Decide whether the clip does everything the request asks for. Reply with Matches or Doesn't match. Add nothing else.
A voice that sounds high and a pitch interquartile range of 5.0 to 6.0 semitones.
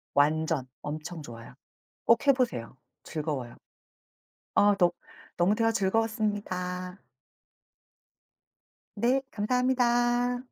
Doesn't match